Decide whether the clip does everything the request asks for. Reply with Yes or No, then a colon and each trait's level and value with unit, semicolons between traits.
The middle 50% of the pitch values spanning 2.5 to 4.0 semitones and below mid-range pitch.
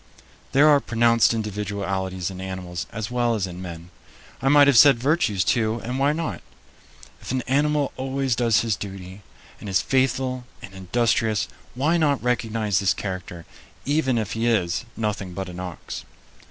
No: wide, 5.4 semitones; low, 115 Hz